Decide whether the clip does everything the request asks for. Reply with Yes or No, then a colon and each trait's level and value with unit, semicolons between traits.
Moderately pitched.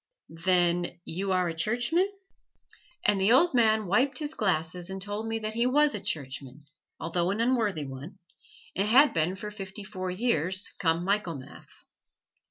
No: high, 195 Hz